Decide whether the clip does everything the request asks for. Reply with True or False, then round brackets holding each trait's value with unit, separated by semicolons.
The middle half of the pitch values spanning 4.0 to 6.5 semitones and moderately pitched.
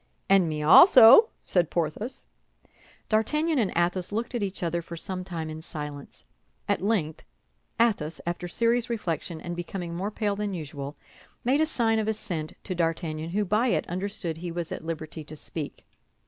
True (5.0 semitones; 180 Hz)